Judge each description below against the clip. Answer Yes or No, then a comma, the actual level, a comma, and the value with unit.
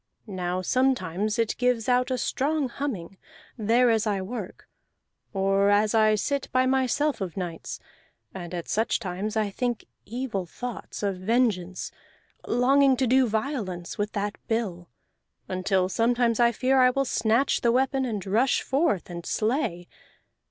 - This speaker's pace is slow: No, average, 150 wpm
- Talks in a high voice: Yes, high, 225 Hz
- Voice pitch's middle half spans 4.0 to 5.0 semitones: Yes, average, 4.7 semitones